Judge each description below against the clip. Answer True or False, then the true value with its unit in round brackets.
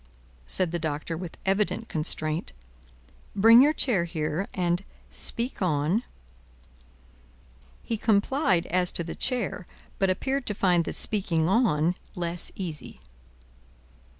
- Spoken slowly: True (120 wpm)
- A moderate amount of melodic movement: True (4.4 semitones)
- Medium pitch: True (180 Hz)